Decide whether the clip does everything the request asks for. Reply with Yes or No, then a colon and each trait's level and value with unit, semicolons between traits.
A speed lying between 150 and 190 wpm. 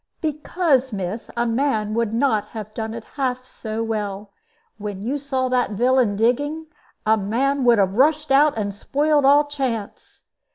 Yes: average, 160 wpm